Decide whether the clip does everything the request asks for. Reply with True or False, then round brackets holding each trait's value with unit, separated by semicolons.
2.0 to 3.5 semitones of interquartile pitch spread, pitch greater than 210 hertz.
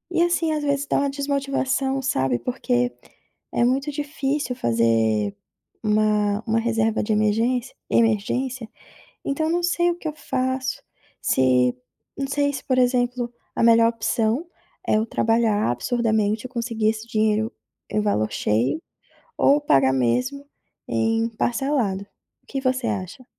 False (4.2 semitones; 235 Hz)